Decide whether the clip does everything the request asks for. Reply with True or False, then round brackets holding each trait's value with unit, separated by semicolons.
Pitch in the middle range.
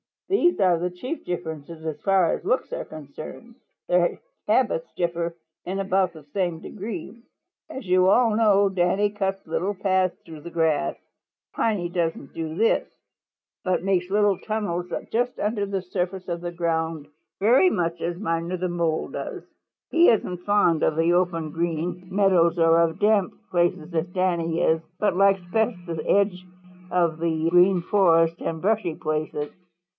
True (180 Hz)